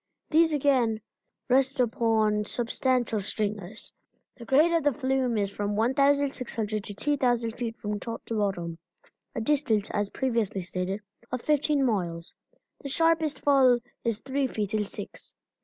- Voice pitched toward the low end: No, high, 235 Hz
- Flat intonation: No, average, 4.5 semitones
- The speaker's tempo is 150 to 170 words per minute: No, average, 140 wpm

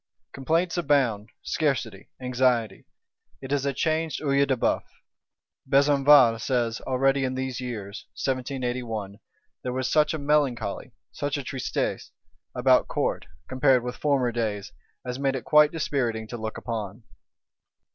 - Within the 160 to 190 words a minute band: No, slow, 135 wpm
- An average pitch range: Yes, average, 3.0 semitones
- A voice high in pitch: No, low, 130 Hz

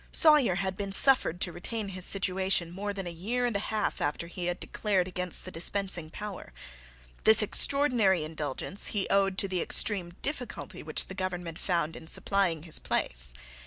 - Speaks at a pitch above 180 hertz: Yes, high, 190 Hz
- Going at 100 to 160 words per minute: No, average, 175 wpm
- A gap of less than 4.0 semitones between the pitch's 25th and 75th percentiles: Yes, average, 2.9 semitones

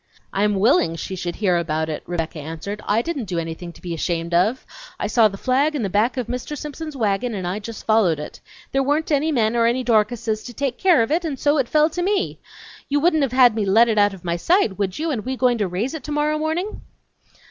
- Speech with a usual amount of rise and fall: No, wide, 7.0 semitones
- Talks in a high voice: Yes, high, 230 Hz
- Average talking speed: No, fast, 245 wpm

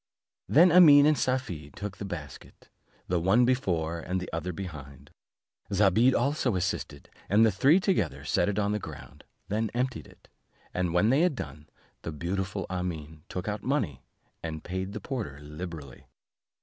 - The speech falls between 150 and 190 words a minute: Yes, average, 160 wpm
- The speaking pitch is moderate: No, very low, 95 Hz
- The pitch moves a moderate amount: No, wide, 6.7 semitones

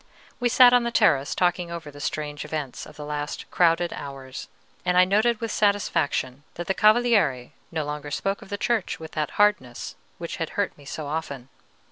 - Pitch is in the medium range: Yes, medium, 165 Hz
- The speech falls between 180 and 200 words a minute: Yes, average, 190 wpm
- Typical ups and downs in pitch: No, wide, 5.7 semitones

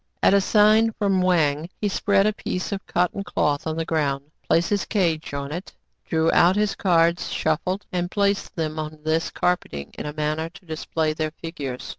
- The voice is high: No, medium, 165 Hz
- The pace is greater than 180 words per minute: Yes, average, 200 wpm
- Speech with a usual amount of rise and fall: Yes, average, 3.8 semitones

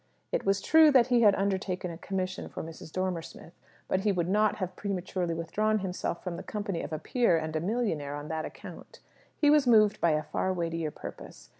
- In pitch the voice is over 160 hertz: Yes, medium, 185 Hz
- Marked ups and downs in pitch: No, average, 4.2 semitones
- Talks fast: Yes, fast, 210 wpm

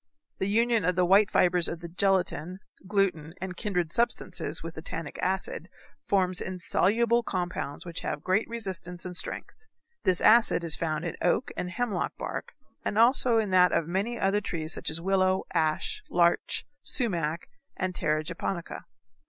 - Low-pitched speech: No, medium, 185 Hz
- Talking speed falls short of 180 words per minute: Yes, average, 160 wpm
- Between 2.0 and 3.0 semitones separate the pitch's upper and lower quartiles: No, average, 3.4 semitones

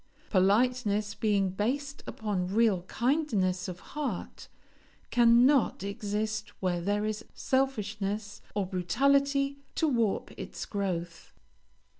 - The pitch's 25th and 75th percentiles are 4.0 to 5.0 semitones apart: Yes, average, 4.5 semitones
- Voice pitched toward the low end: No, high, 210 Hz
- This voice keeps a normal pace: No, slow, 100 wpm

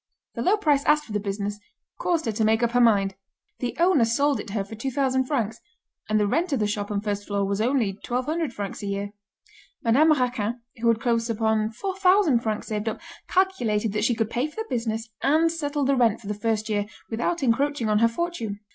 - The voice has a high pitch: Yes, high, 230 Hz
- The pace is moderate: No, fast, 220 wpm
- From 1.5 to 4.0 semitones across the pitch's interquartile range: No, average, 5.1 semitones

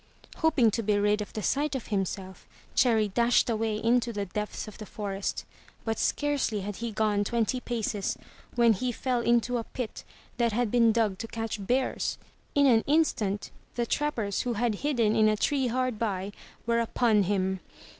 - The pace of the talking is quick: No, average, 180 wpm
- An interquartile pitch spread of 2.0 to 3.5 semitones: Yes, average, 2.8 semitones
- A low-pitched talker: No, high, 225 Hz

